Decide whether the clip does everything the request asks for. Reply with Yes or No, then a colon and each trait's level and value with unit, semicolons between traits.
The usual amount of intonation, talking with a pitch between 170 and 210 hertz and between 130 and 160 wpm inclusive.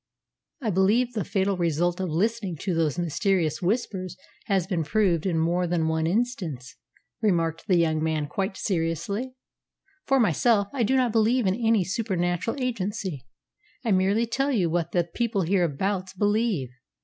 Yes: average, 4.7 semitones; high, 190 Hz; average, 155 wpm